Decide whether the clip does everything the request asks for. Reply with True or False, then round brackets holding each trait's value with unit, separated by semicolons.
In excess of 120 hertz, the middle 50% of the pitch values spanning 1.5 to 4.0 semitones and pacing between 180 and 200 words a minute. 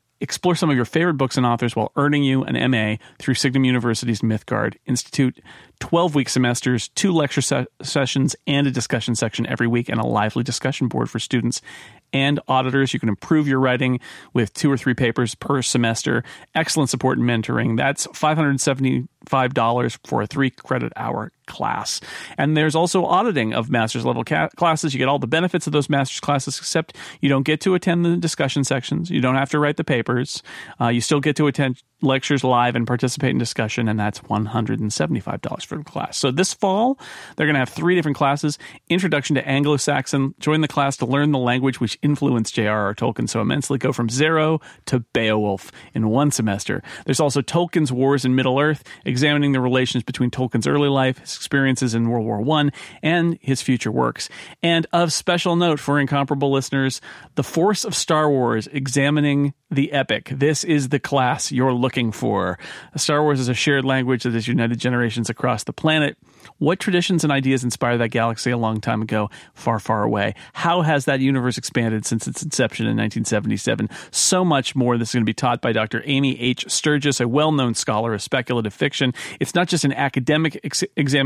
True (135 Hz; 3.6 semitones; 190 wpm)